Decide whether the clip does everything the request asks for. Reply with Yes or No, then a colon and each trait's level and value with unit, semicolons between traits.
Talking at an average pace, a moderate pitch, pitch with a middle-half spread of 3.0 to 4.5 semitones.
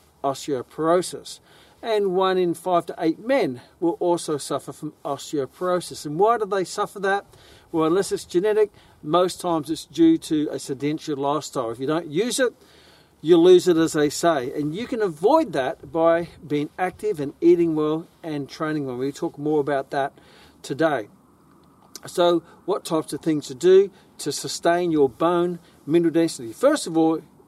Yes: average, 170 wpm; medium, 165 Hz; average, 3.6 semitones